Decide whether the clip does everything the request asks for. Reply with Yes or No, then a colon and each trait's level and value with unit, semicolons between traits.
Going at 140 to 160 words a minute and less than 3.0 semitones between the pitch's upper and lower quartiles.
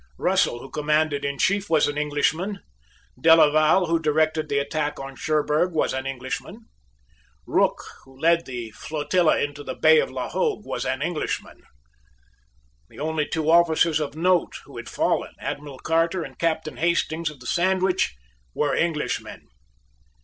Yes: average, 150 wpm; narrow, 2.5 semitones